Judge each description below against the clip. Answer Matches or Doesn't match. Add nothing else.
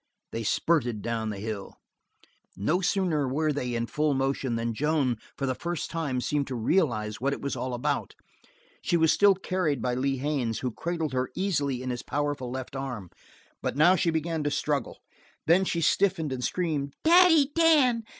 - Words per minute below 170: Doesn't match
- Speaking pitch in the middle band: Matches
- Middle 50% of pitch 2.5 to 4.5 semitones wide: Doesn't match